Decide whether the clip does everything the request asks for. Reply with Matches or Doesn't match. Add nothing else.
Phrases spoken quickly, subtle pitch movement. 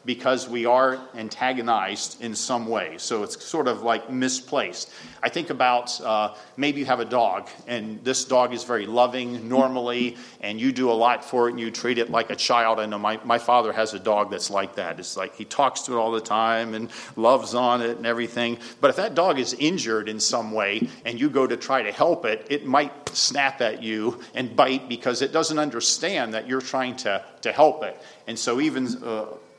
Matches